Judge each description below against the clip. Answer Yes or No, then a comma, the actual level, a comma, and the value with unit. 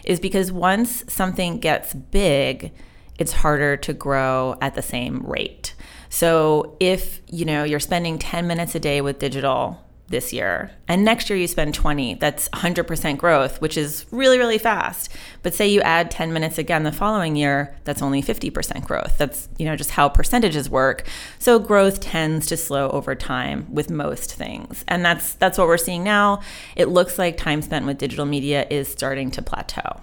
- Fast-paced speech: No, average, 185 wpm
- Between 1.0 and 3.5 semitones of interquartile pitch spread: No, average, 4.5 semitones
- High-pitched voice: No, medium, 160 Hz